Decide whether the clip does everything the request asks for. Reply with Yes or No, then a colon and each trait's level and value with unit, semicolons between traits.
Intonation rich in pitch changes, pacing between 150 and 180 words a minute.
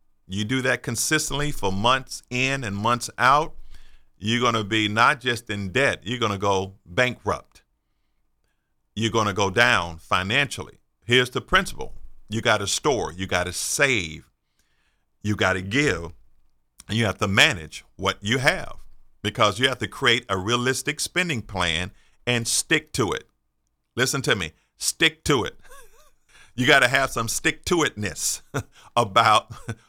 No: average, 4.4 semitones; average, 160 wpm